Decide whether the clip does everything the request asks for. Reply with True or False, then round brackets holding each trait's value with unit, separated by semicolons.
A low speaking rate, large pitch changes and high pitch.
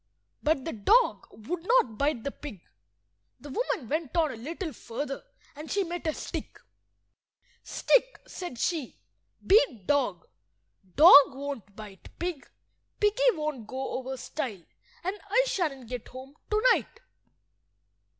True (130 wpm; 5.9 semitones; 290 Hz)